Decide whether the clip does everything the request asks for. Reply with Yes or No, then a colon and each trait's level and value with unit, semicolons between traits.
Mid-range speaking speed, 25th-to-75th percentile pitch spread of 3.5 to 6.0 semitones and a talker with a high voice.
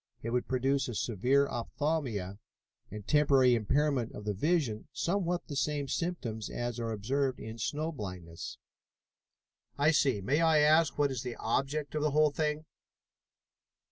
No: average, 150 wpm; average, 4.7 semitones; low, 135 Hz